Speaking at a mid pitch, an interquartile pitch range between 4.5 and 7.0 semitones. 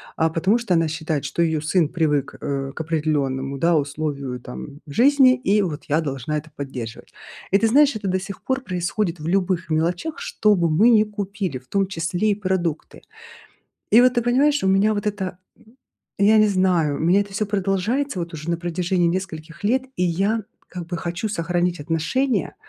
Yes: medium, 180 Hz; average, 4.8 semitones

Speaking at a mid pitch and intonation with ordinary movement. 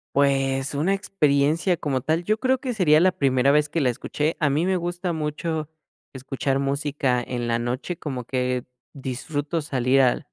Yes: medium, 145 Hz; average, 3.8 semitones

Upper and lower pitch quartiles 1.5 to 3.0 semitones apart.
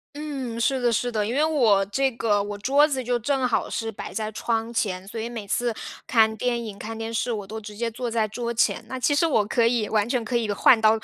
Yes: narrow, 2.4 semitones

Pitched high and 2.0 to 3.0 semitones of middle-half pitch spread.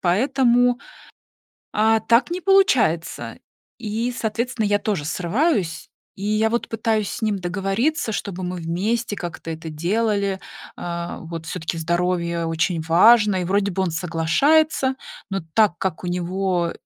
No: high, 195 Hz; average, 4.8 semitones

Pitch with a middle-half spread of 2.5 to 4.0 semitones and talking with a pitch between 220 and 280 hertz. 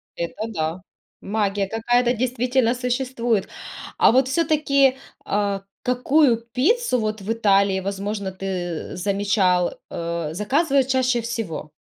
No: average, 4.5 semitones; high, 225 Hz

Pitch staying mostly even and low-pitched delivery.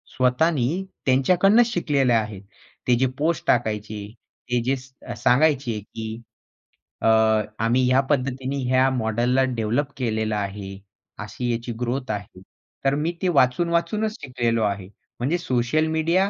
No: average, 4.4 semitones; low, 125 Hz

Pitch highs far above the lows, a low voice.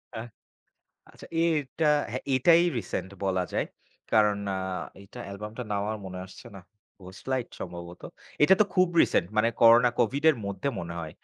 Yes: wide, 5.7 semitones; low, 110 Hz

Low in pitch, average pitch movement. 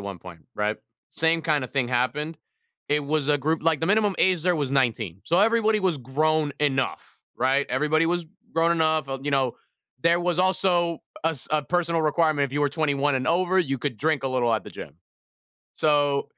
No: medium, 150 Hz; average, 3.7 semitones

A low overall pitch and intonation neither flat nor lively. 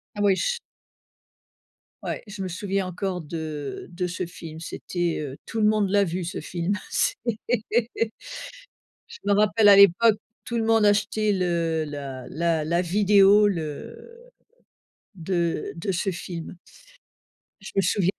No: medium, 185 Hz; average, 3.7 semitones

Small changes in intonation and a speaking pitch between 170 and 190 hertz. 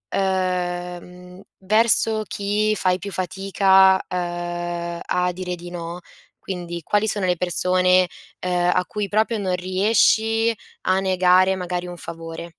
Yes: narrow, 1.7 semitones; medium, 185 Hz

